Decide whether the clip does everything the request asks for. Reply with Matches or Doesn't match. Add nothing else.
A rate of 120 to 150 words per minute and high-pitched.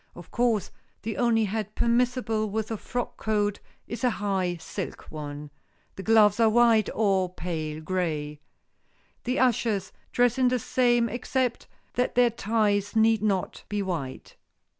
Matches